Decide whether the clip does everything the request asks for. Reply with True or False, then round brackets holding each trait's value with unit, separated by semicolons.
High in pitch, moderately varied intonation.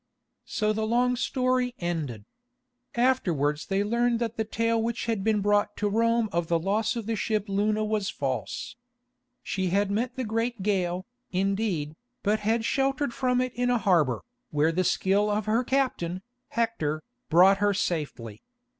True (210 Hz; 4.1 semitones)